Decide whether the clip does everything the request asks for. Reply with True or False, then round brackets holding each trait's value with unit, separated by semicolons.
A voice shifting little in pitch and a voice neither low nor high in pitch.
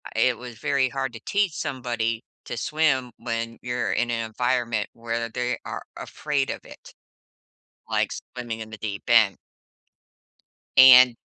False (2.1 semitones; 120 Hz)